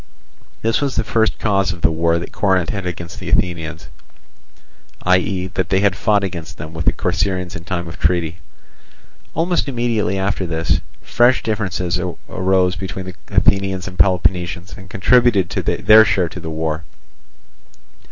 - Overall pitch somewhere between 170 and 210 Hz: No, very low, 95 Hz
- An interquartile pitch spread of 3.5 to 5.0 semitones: No, average, 2.7 semitones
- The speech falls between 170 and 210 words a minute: No, average, 155 wpm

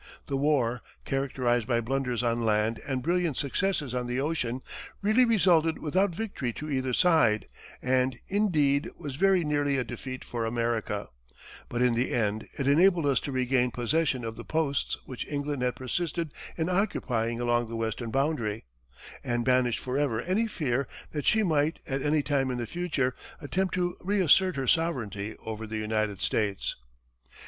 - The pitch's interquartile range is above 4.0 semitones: Yes, average, 5.1 semitones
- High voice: No, low, 135 Hz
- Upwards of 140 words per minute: Yes, average, 165 wpm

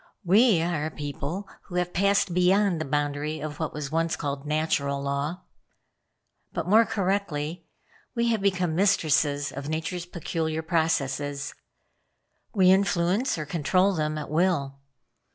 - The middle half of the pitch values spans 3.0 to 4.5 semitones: Yes, average, 4.0 semitones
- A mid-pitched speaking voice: Yes, medium, 160 Hz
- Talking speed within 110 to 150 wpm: Yes, slow, 135 wpm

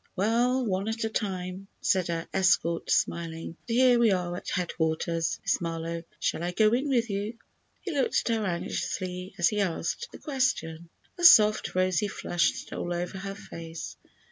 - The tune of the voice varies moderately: Yes, average, 4.7 semitones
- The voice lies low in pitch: No, high, 190 Hz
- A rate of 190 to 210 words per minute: No, average, 170 wpm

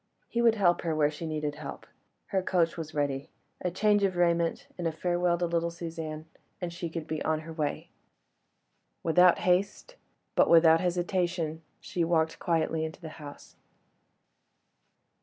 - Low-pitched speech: No, medium, 170 Hz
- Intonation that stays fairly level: Yes, narrow, 2.0 semitones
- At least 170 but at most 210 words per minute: No, average, 160 wpm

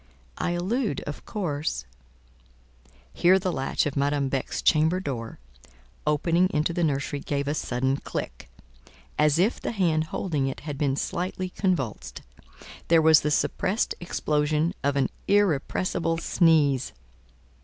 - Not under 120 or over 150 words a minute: Yes, slow, 135 wpm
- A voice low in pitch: No, medium, 155 Hz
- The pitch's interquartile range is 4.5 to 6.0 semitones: No, average, 3.8 semitones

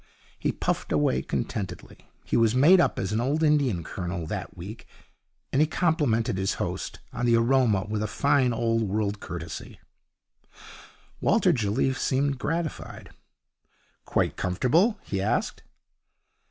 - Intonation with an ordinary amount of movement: No, wide, 5.9 semitones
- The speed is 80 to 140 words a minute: Yes, slow, 135 wpm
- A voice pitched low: Yes, low, 115 Hz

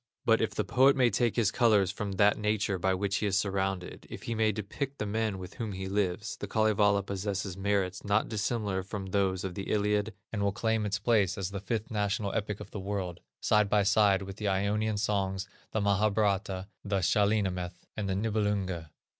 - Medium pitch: No, low, 100 Hz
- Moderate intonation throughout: No, narrow, 1.8 semitones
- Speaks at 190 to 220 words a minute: Yes, fast, 205 wpm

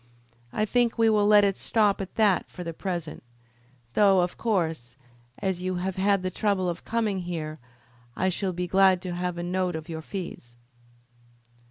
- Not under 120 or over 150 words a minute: No, average, 180 wpm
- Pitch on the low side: No, medium, 185 Hz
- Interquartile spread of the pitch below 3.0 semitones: Yes, narrow, 2.5 semitones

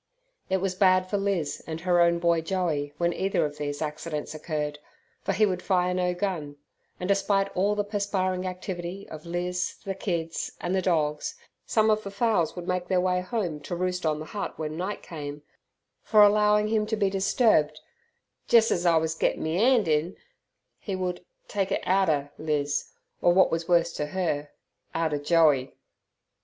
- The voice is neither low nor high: Yes, medium, 180 Hz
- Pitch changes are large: No, average, 3.6 semitones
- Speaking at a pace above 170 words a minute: Yes, average, 180 wpm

